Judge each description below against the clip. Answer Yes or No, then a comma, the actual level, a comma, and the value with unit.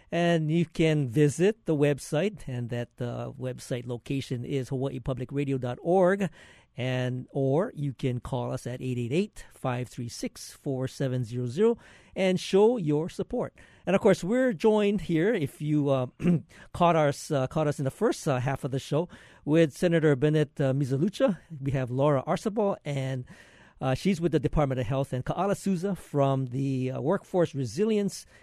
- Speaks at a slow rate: No, average, 155 wpm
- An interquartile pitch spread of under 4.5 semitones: No, average, 5.1 semitones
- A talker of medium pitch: Yes, medium, 145 Hz